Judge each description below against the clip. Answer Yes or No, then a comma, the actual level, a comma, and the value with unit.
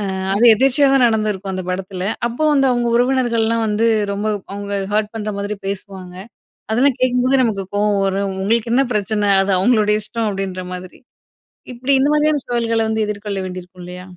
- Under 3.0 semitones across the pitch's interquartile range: No, average, 3.6 semitones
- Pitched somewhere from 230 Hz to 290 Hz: No, high, 215 Hz